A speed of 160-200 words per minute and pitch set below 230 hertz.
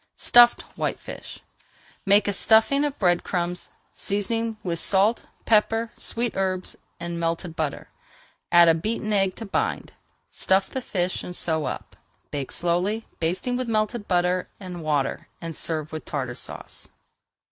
No: average, 145 wpm; medium, 185 Hz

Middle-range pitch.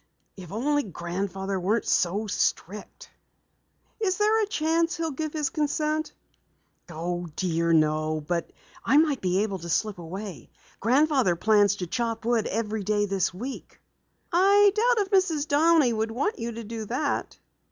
No: high, 225 Hz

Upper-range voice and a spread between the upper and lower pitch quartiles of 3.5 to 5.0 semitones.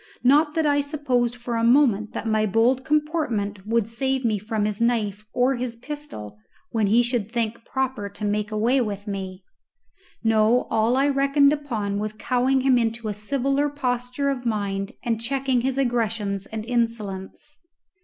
Yes: high, 235 Hz; average, 3.9 semitones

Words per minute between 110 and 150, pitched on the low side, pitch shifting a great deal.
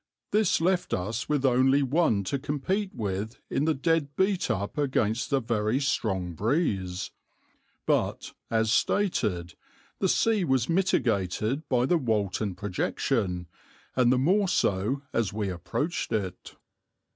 Yes: slow, 135 wpm; low, 125 Hz; wide, 6.9 semitones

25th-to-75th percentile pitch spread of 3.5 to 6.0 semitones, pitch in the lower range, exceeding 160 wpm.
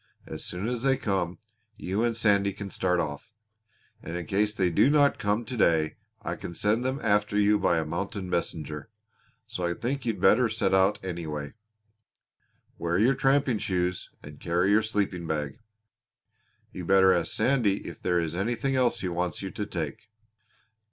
Yes: average, 4.4 semitones; low, 100 Hz; average, 175 wpm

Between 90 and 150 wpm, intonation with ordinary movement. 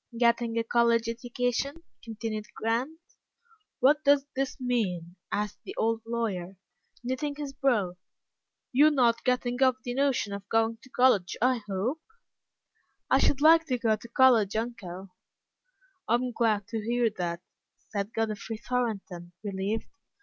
Yes: slow, 135 wpm; average, 3.3 semitones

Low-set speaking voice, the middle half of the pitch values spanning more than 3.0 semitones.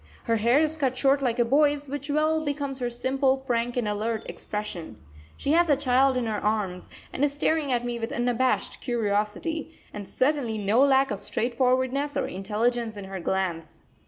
No: high, 245 Hz; average, 4.4 semitones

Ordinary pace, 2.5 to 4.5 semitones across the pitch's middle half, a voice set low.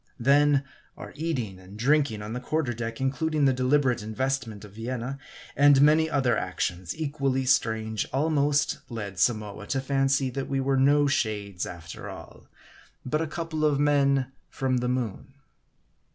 Yes: average, 150 wpm; average, 4.2 semitones; low, 130 Hz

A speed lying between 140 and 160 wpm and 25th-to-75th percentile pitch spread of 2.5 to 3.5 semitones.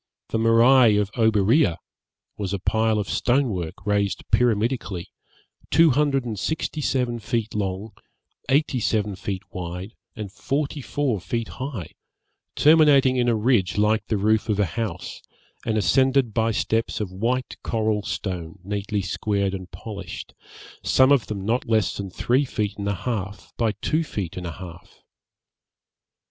No: average, 155 wpm; average, 3.9 semitones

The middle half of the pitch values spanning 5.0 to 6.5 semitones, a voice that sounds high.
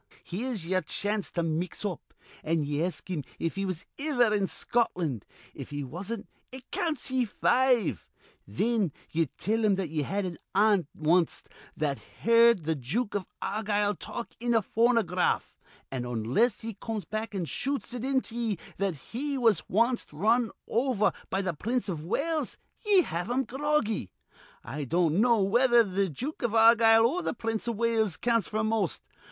Yes: average, 5.3 semitones; high, 215 Hz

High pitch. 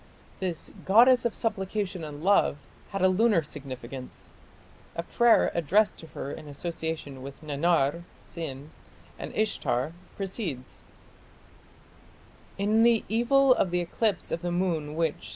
No: medium, 175 Hz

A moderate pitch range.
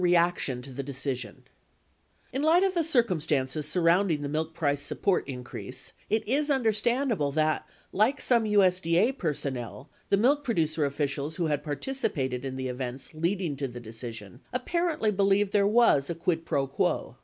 No: wide, 7.6 semitones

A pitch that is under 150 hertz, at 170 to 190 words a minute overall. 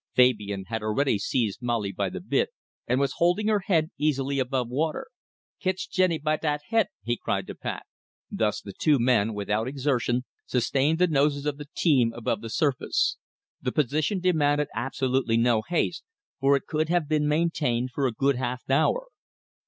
Yes: low, 135 Hz; average, 175 wpm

